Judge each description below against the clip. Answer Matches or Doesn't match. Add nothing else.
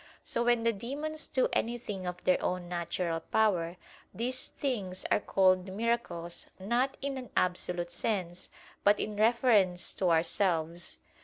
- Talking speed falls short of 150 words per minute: Matches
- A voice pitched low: Doesn't match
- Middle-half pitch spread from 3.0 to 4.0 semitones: Doesn't match